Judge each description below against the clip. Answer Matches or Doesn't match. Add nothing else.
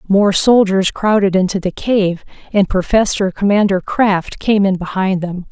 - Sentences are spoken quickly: Doesn't match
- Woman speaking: Matches